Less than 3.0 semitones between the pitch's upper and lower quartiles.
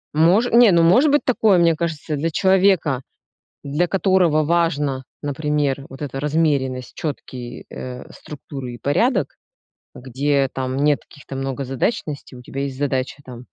No: average, 4.0 semitones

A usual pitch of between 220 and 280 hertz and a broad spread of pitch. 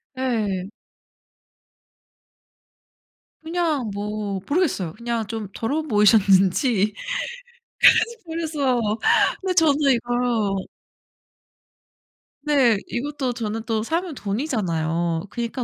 Yes: high, 235 Hz; wide, 5.8 semitones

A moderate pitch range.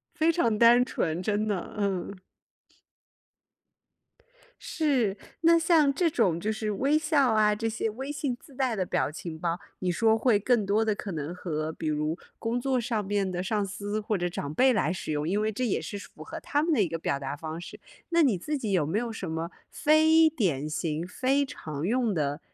No: wide, 6.7 semitones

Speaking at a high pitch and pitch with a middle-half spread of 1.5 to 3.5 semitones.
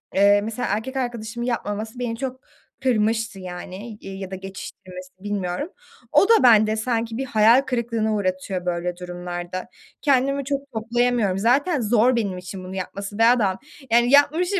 No: high, 220 Hz; average, 4.4 semitones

